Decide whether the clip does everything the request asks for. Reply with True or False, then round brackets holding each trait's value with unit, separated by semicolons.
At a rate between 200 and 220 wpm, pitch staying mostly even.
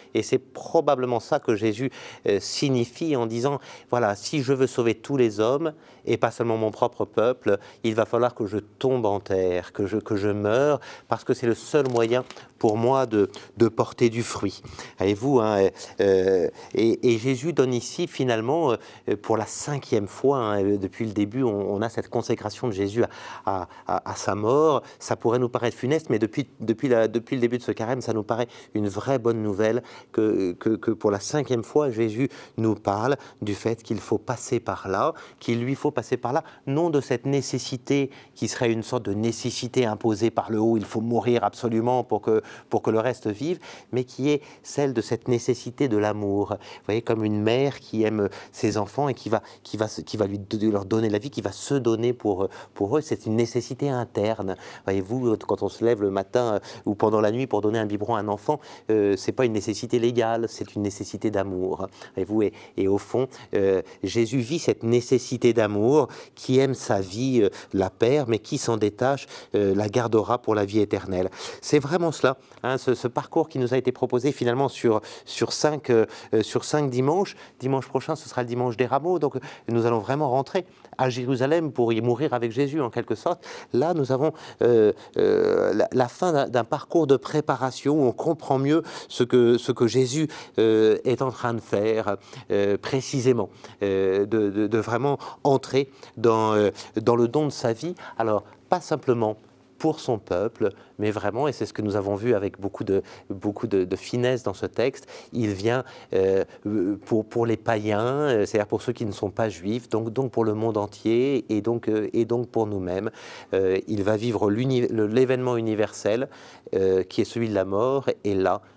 False (205 wpm; 3.7 semitones)